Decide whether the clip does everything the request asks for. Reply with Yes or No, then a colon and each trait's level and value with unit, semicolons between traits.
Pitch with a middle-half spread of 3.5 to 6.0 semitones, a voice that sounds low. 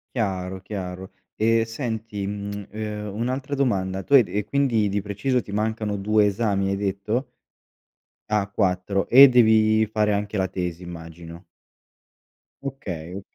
No: narrow, 2.5 semitones; low, 105 Hz